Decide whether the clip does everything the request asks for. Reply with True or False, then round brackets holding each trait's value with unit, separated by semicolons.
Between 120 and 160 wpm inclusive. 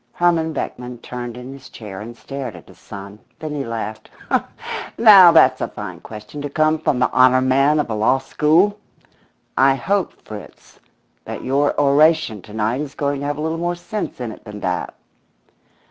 False (185 wpm)